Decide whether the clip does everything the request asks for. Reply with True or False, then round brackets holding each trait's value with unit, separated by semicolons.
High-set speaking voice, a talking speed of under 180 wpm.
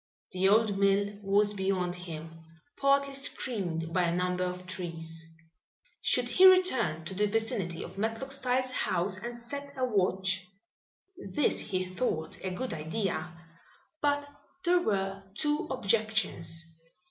True (195 Hz; 135 wpm)